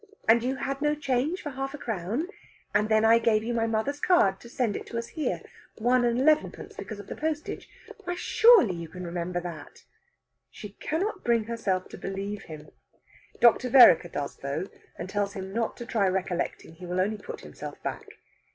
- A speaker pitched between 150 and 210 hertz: No, high, 225 Hz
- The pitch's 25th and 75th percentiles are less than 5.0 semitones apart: No, wide, 5.6 semitones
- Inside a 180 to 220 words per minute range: Yes, average, 195 wpm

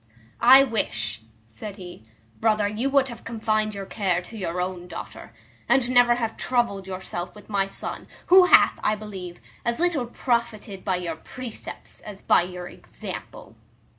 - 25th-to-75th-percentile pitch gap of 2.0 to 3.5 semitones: No, average, 4.6 semitones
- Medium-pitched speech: No, high, 210 Hz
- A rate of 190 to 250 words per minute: No, average, 160 wpm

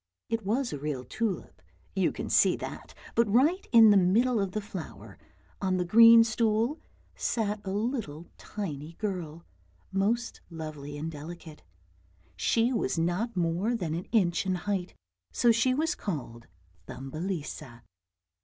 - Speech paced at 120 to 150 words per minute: Yes, average, 145 wpm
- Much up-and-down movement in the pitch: Yes, wide, 5.8 semitones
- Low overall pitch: No, high, 195 Hz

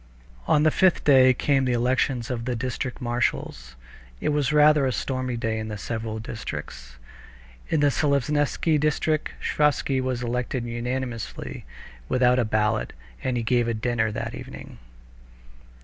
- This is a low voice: Yes, low, 125 Hz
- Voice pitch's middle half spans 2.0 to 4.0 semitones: Yes, average, 3.2 semitones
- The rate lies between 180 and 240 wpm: No, average, 145 wpm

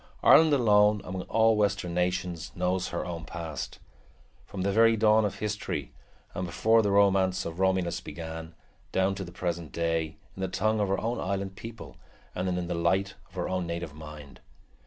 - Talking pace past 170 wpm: Yes, average, 180 wpm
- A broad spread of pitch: No, average, 3.2 semitones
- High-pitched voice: No, very low, 95 Hz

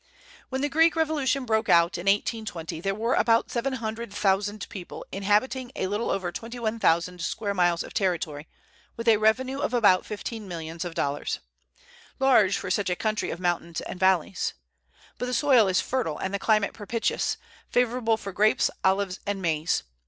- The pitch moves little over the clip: No, average, 4.3 semitones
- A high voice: Yes, high, 205 Hz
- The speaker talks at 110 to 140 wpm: No, average, 175 wpm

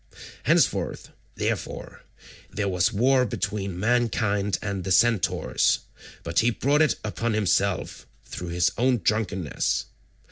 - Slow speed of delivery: Yes, slow, 115 wpm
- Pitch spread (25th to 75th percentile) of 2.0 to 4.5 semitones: Yes, average, 4.1 semitones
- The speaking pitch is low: Yes, low, 105 Hz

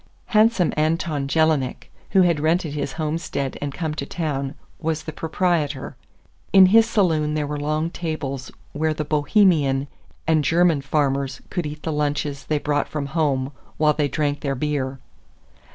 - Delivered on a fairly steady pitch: Yes, narrow, 2.3 semitones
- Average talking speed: Yes, average, 155 wpm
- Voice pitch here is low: No, medium, 150 Hz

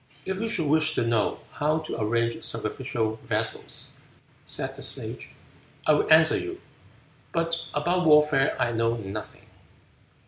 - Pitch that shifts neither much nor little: No, wide, 6.0 semitones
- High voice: No, medium, 150 Hz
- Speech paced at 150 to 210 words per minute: No, average, 140 wpm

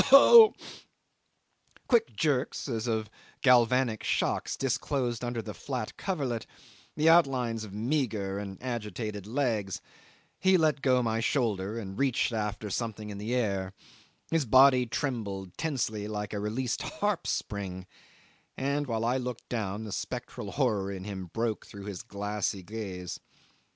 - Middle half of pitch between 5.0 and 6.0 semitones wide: No, average, 4.0 semitones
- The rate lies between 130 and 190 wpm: Yes, average, 140 wpm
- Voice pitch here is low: Yes, low, 115 Hz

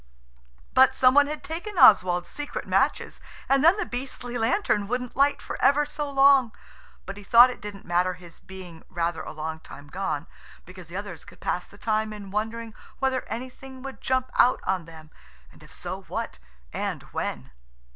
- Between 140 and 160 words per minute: No, average, 180 wpm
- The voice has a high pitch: Yes, high, 220 Hz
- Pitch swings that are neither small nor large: No, wide, 6.8 semitones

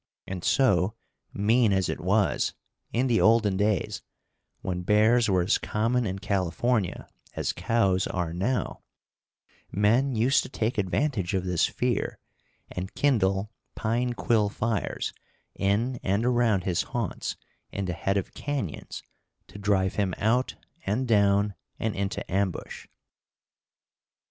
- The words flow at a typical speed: No, slow, 130 wpm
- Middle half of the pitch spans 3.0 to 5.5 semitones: Yes, average, 3.6 semitones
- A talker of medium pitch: No, low, 105 Hz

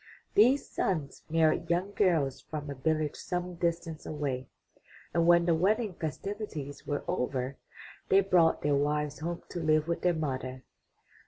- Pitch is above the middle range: No, medium, 160 Hz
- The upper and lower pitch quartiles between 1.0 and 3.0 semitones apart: No, average, 3.4 semitones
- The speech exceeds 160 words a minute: No, average, 150 wpm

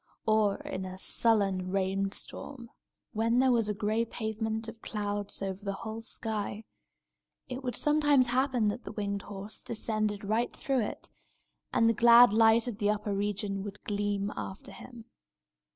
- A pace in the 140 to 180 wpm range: Yes, average, 160 wpm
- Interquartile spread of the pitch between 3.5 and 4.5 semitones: No, narrow, 2.4 semitones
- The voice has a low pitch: No, high, 215 Hz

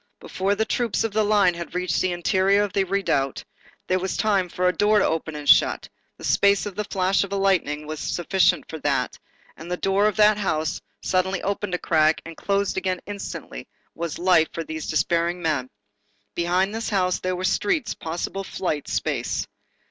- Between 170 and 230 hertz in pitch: Yes, medium, 185 Hz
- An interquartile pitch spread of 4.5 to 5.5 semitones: No, average, 3.0 semitones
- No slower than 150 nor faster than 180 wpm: No, average, 190 wpm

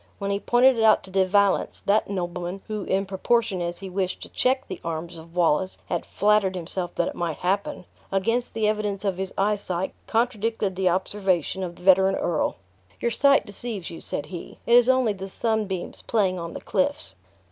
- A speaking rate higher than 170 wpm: Yes, average, 195 wpm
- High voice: Yes, high, 195 Hz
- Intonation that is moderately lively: Yes, average, 3.1 semitones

